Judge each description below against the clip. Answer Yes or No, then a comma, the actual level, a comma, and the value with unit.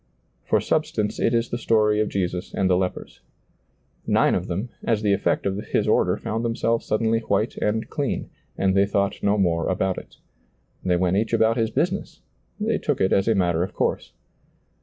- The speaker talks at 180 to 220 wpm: Yes, average, 190 wpm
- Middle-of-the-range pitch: No, low, 105 Hz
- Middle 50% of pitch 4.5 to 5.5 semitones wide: No, average, 3.0 semitones